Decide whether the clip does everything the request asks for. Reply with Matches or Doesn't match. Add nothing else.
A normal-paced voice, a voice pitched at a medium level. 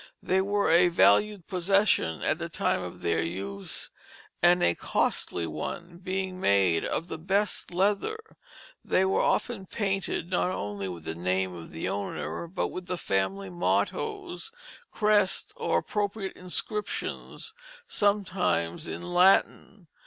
Doesn't match